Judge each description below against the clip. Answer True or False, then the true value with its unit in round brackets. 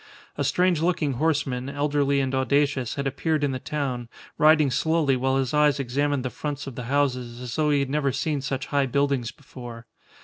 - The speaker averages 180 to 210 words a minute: True (195 wpm)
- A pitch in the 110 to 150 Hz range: True (140 Hz)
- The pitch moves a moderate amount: False (2.3 semitones)